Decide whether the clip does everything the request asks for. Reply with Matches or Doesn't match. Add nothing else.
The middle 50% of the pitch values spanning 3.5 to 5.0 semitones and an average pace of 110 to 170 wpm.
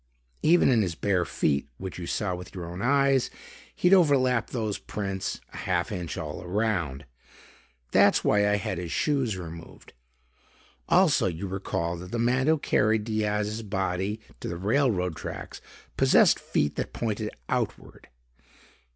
Matches